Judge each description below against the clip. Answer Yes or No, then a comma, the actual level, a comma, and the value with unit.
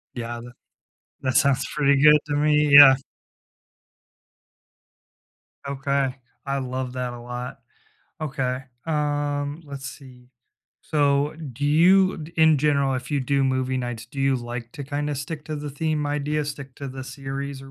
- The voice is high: No, medium, 140 Hz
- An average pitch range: No, narrow, 2.2 semitones